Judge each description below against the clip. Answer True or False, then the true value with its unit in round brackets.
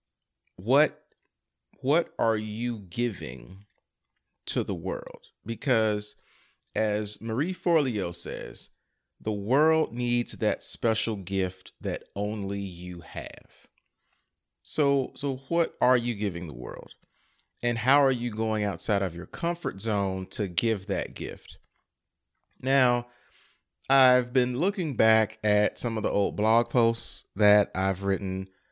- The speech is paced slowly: True (125 wpm)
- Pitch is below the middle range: True (110 Hz)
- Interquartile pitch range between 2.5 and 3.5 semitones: False (3.9 semitones)